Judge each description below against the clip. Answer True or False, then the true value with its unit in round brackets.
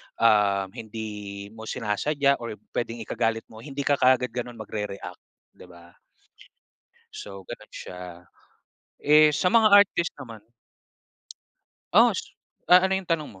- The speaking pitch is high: False (115 Hz)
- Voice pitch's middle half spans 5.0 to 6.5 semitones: True (5.5 semitones)